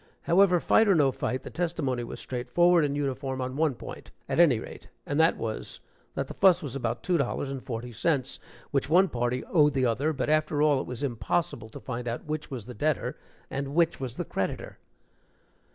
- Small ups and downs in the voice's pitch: No, average, 4.3 semitones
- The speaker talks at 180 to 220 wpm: Yes, average, 200 wpm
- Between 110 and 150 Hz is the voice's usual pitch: Yes, medium, 140 Hz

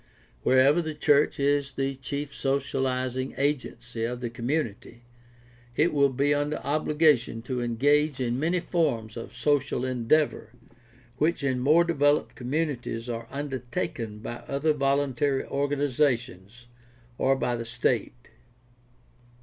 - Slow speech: Yes, slow, 125 wpm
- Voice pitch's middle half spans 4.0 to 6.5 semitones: No, average, 3.2 semitones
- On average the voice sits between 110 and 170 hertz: Yes, low, 135 Hz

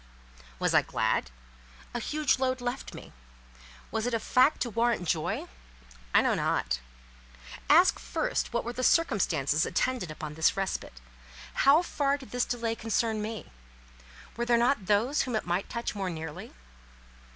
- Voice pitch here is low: No, high, 235 Hz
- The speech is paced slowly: No, average, 155 wpm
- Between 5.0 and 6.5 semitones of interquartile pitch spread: Yes, average, 5.3 semitones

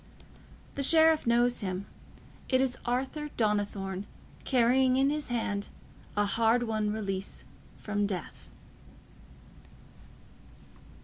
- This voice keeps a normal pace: No, slow, 100 wpm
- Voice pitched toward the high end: Yes, high, 230 Hz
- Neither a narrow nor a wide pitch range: Yes, average, 4.3 semitones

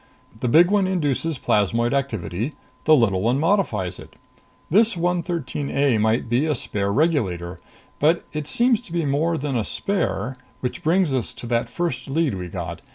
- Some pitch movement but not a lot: No, wide, 6.7 semitones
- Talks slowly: No, average, 170 wpm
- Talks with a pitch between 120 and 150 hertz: Yes, medium, 140 Hz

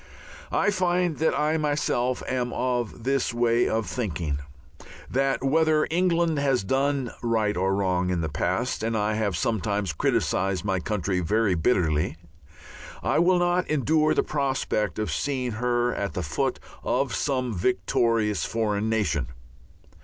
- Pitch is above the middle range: No, low, 115 Hz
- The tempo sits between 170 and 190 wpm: No, average, 145 wpm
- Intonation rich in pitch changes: Yes, wide, 5.9 semitones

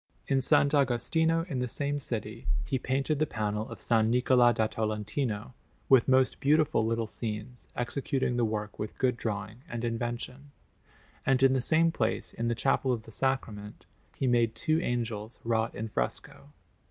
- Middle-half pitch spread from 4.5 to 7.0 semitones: No, average, 3.3 semitones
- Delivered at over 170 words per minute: No, average, 165 wpm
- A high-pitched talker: No, low, 120 Hz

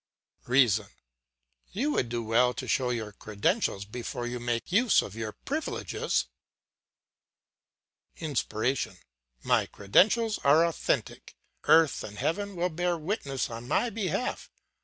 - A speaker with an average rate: No, slow, 120 wpm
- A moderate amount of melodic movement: No, wide, 7.9 semitones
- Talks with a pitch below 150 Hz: Yes, low, 135 Hz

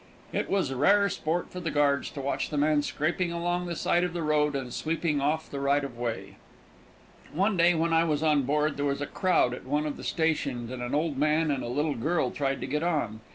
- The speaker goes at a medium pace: No, fast, 240 wpm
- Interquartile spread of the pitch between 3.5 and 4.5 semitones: No, average, 3.1 semitones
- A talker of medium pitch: Yes, medium, 150 Hz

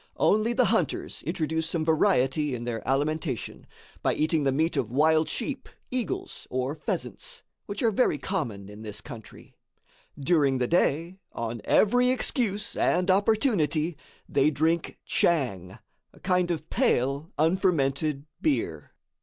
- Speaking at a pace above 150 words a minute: No, slow, 135 wpm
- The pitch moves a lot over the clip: Yes, wide, 5.8 semitones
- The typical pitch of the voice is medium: Yes, medium, 160 Hz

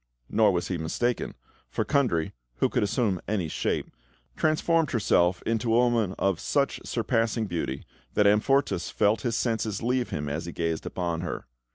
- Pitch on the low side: Yes, low, 105 Hz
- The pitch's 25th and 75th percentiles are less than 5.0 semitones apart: No, average, 5.3 semitones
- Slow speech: No, average, 165 wpm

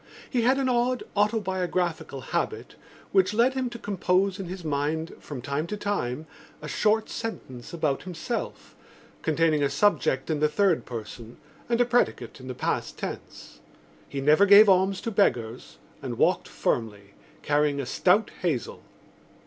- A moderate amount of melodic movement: No, wide, 6.8 semitones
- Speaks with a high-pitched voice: No, medium, 175 Hz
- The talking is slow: No, average, 155 wpm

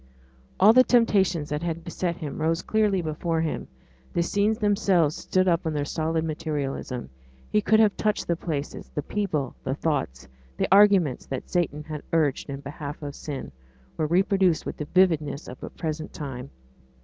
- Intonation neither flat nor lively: Yes, average, 4.3 semitones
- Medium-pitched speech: Yes, medium, 160 Hz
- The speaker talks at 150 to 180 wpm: Yes, average, 175 wpm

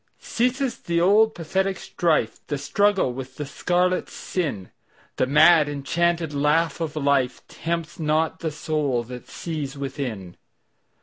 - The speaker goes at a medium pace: No, slow, 115 wpm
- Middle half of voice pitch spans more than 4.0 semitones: No, average, 3.7 semitones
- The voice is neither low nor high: Yes, medium, 155 Hz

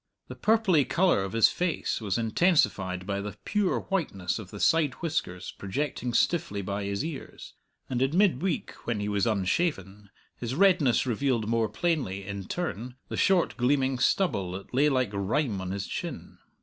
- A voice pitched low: Yes, low, 120 Hz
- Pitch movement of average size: No, wide, 8.2 semitones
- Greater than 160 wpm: Yes, average, 170 wpm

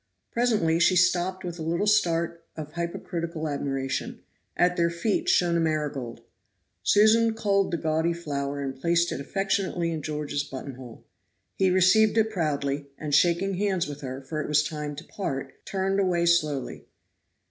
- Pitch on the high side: No, medium, 170 Hz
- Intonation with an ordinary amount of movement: Yes, average, 4.2 semitones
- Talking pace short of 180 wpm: Yes, average, 160 wpm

